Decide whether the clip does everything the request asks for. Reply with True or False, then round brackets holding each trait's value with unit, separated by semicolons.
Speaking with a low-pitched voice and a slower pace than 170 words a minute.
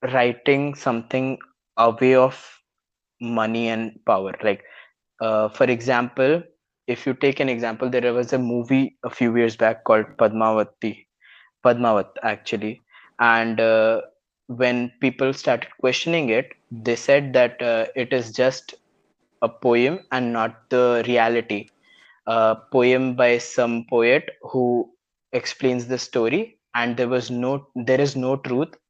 True (125 Hz; 135 wpm)